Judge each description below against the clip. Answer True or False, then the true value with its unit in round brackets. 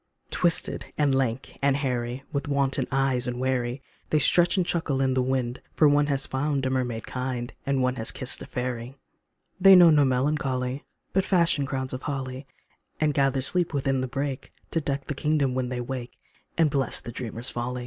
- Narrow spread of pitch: True (2.2 semitones)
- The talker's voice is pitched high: False (135 Hz)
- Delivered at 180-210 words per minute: True (190 wpm)